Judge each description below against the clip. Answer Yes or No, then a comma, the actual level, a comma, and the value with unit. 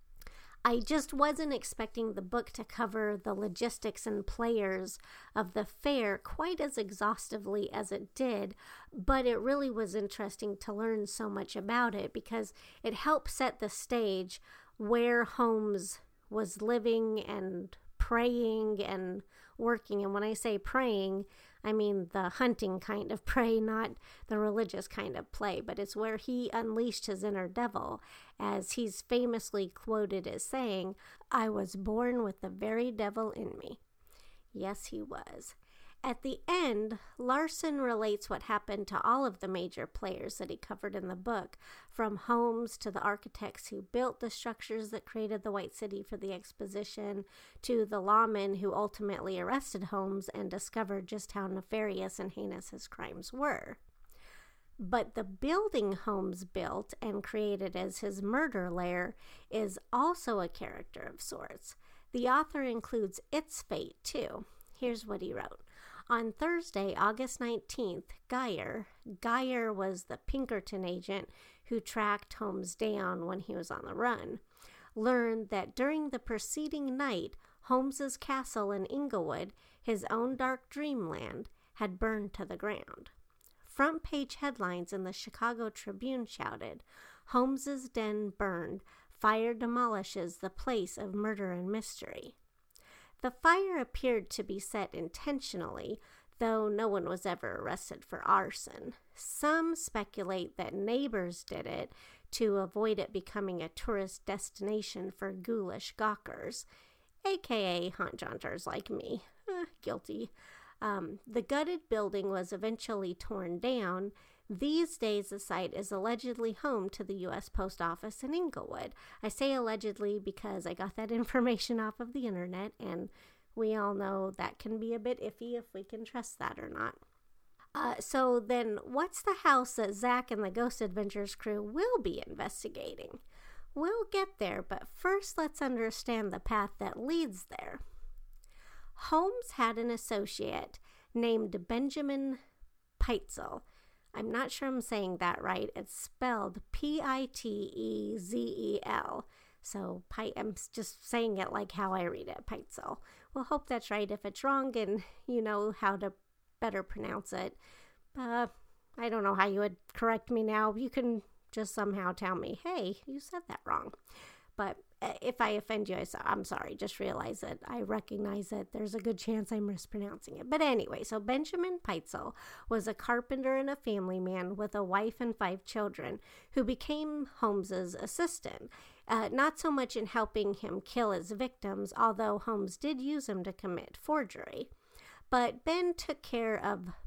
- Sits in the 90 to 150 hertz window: No, high, 220 Hz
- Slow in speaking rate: No, average, 155 wpm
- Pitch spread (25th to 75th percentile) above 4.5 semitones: No, average, 3.7 semitones